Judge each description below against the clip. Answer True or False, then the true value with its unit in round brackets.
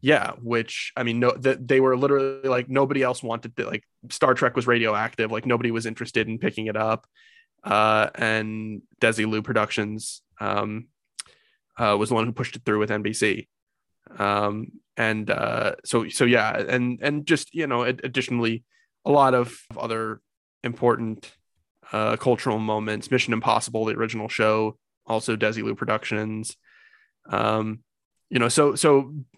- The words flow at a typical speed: True (155 wpm)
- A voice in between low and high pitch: False (115 Hz)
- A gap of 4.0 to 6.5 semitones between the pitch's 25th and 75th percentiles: False (2.7 semitones)